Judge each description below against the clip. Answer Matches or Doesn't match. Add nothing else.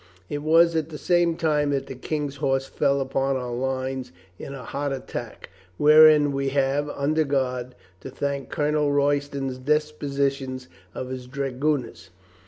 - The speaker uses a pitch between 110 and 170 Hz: Matches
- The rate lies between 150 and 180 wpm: Matches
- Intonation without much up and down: Matches